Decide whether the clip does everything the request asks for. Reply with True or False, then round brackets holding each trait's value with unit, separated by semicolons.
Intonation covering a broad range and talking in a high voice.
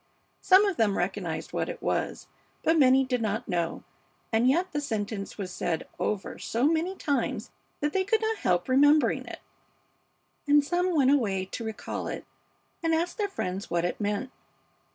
True (8.1 semitones; 265 Hz)